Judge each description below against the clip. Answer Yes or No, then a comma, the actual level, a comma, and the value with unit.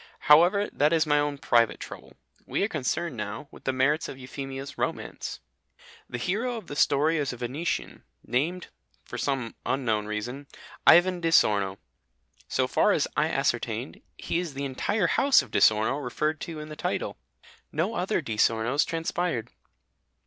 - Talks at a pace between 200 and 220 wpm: No, average, 165 wpm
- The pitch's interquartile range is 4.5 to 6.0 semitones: Yes, average, 5.2 semitones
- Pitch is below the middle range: No, medium, 145 Hz